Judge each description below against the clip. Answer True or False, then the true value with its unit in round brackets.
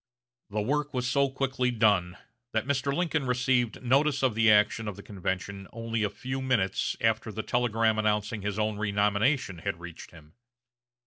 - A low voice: True (110 Hz)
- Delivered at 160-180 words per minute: True (170 wpm)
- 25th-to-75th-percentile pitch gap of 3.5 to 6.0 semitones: True (3.9 semitones)